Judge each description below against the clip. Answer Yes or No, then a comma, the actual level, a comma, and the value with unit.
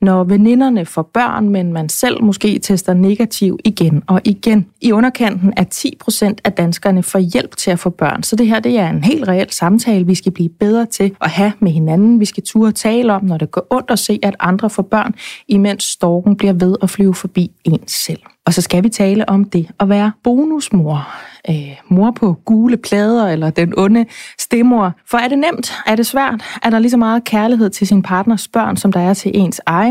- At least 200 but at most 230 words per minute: Yes, average, 220 wpm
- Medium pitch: No, high, 205 Hz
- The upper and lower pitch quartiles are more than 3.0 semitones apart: Yes, average, 3.5 semitones